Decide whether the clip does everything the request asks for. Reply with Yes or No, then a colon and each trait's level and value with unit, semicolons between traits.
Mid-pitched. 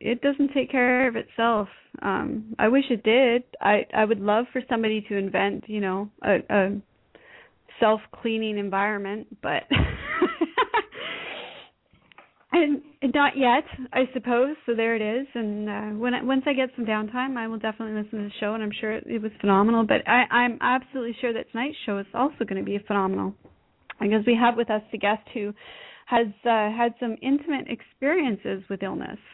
No: high, 230 Hz